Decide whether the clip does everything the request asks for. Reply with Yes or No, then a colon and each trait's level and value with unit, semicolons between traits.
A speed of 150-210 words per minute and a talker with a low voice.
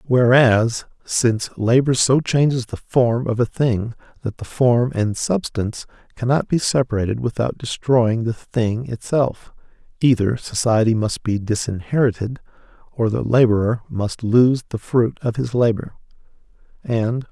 No: slow, 135 wpm; low, 120 Hz